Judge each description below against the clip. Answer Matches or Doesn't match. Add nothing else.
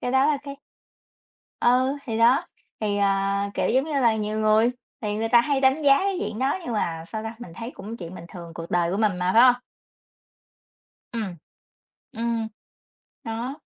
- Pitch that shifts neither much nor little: Matches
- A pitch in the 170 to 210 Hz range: Doesn't match